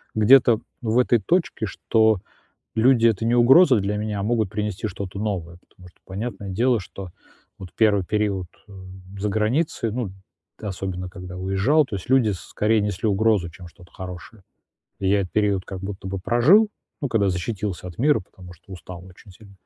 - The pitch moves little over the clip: No, average, 3.2 semitones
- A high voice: No, low, 105 Hz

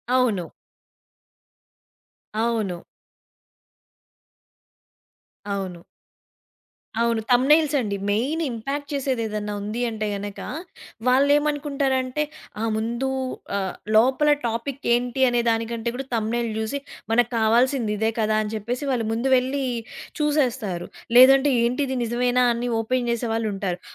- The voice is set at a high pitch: Yes, high, 235 Hz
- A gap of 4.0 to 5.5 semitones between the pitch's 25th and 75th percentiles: No, average, 3.2 semitones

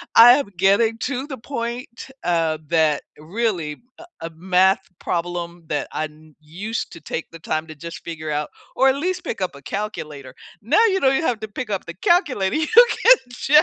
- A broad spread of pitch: Yes, wide, 7.3 semitones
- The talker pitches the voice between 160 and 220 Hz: Yes, high, 190 Hz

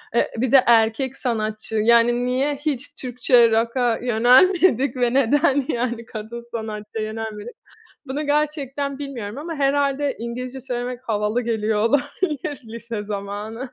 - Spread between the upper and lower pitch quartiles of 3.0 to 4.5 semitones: Yes, average, 3.6 semitones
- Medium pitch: No, high, 245 Hz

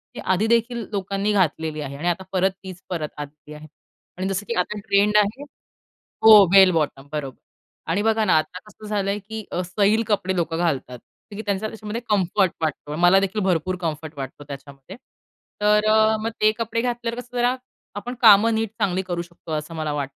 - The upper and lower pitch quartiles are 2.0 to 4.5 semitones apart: No, average, 4.9 semitones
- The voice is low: No, high, 190 Hz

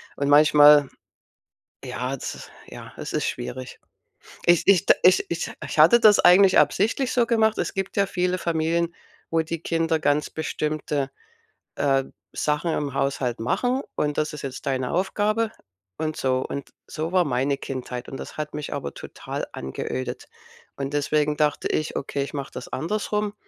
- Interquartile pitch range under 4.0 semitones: No, average, 4.6 semitones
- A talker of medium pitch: Yes, medium, 150 Hz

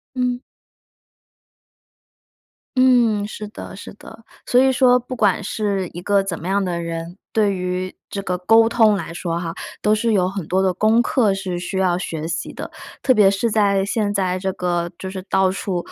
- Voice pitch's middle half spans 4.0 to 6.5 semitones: No, average, 3.2 semitones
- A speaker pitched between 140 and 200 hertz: Yes, high, 195 Hz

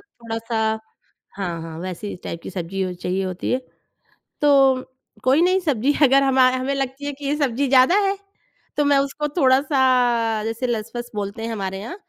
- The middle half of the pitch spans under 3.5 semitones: No, average, 4.4 semitones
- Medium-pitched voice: No, very high, 255 Hz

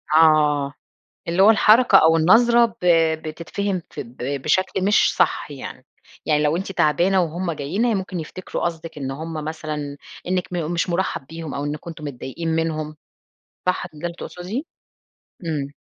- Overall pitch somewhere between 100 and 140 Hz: No, medium, 165 Hz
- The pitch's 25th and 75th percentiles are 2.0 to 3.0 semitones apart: No, average, 3.5 semitones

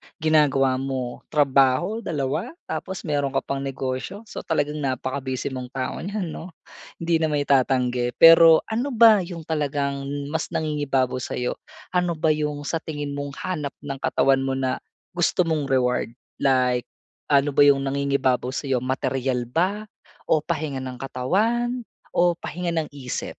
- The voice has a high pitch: No, medium, 140 Hz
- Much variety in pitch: No, average, 3.8 semitones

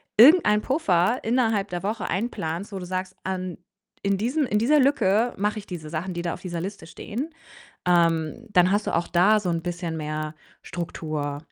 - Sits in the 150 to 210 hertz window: Yes, medium, 185 Hz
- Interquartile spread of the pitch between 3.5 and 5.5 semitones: Yes, average, 4.0 semitones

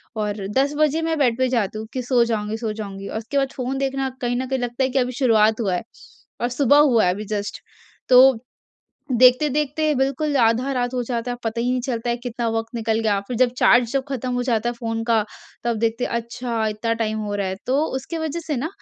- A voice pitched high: Yes, high, 245 Hz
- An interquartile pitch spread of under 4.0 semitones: Yes, average, 2.9 semitones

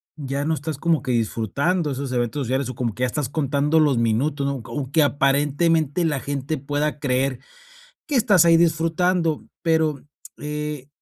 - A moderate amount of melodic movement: Yes, average, 3.2 semitones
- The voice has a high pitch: No, medium, 145 Hz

